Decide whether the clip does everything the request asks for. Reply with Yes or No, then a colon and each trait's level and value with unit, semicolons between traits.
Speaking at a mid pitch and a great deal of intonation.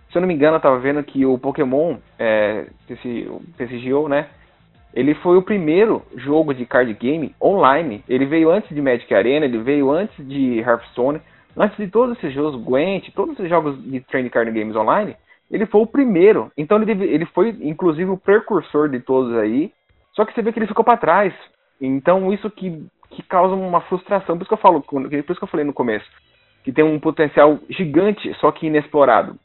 Yes: medium, 155 Hz; wide, 6.1 semitones